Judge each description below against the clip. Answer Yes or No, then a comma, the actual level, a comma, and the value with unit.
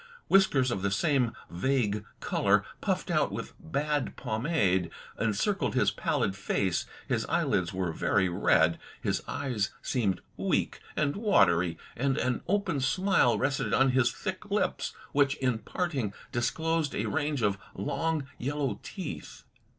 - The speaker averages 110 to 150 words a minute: Yes, slow, 135 wpm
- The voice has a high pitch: No, low, 125 Hz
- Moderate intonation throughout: No, wide, 6.8 semitones